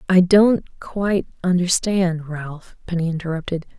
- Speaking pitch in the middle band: Yes, medium, 175 Hz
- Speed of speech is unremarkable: No, slow, 95 wpm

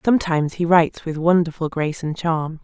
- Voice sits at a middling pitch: Yes, medium, 165 Hz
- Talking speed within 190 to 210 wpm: No, average, 180 wpm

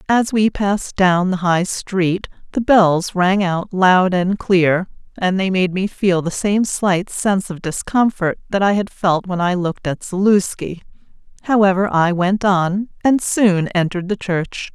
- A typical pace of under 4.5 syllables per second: Yes, 4.1 syllables/s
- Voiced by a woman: Yes, female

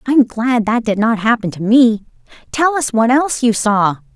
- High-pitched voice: Yes, high, 235 Hz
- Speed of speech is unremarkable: No, fast, 215 wpm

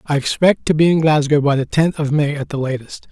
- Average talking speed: No, fast, 270 wpm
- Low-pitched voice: No, medium, 150 Hz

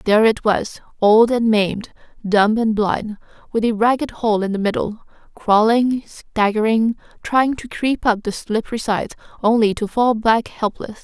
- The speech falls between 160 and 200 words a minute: Yes, average, 165 wpm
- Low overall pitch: No, high, 220 Hz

